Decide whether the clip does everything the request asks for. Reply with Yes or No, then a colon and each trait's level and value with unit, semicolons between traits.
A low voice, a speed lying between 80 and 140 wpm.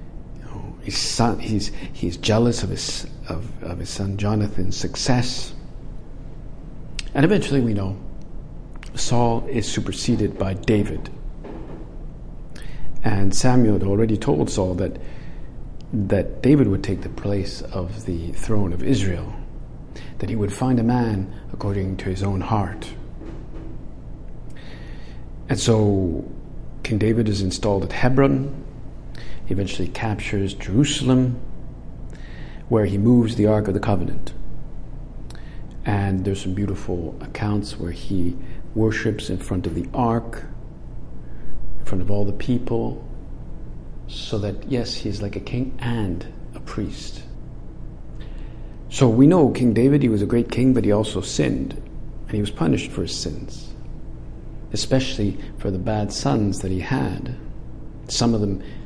Yes: low, 105 Hz; slow, 135 wpm